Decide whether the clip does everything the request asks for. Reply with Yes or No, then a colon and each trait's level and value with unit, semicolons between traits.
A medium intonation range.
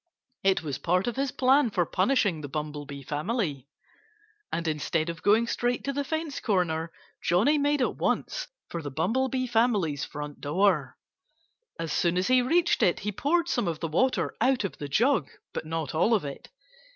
No: wide, 8.4 semitones